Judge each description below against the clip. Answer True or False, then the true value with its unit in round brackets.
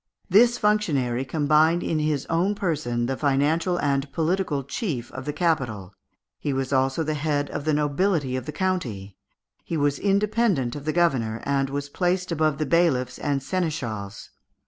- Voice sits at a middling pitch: True (150 Hz)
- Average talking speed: True (165 wpm)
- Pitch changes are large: False (4.4 semitones)